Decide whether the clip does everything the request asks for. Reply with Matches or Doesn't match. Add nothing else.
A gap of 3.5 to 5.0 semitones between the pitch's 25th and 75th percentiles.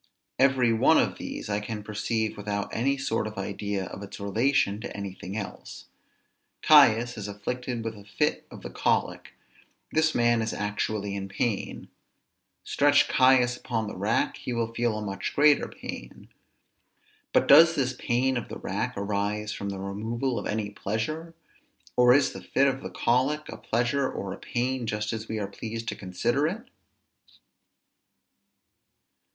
Matches